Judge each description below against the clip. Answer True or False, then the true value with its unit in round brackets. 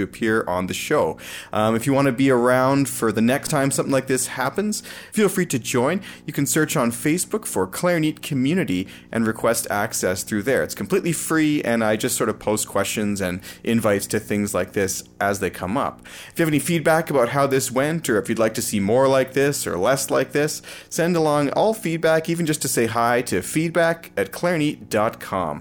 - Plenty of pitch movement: True (6.3 semitones)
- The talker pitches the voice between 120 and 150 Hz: True (135 Hz)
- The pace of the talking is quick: True (210 wpm)